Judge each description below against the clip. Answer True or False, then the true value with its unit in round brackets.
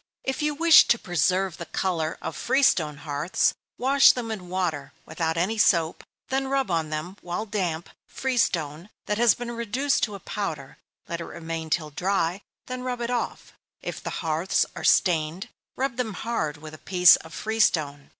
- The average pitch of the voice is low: False (185 Hz)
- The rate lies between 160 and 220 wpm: True (185 wpm)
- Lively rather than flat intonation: True (6.6 semitones)